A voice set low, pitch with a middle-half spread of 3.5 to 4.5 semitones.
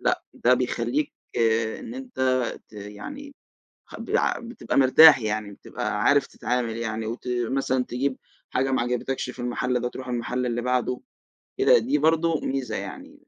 Yes: low, 125 Hz; average, 3.9 semitones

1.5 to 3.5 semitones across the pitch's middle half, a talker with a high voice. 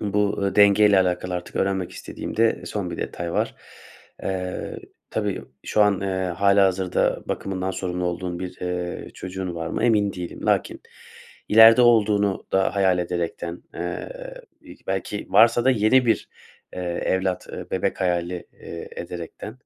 No: narrow, 2.5 semitones; very low, 95 Hz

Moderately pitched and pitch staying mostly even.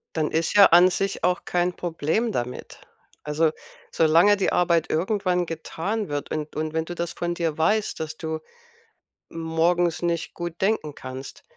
Yes: medium, 170 Hz; narrow, 2.1 semitones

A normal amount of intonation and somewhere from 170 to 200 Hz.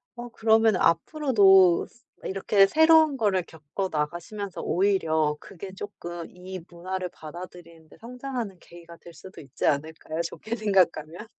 Yes: average, 4.4 semitones; medium, 185 Hz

